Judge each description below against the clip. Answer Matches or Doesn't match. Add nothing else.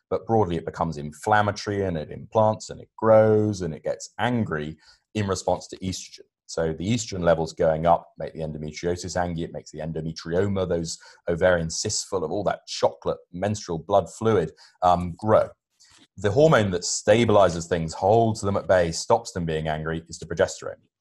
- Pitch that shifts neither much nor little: Matches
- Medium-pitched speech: Doesn't match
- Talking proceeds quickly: Doesn't match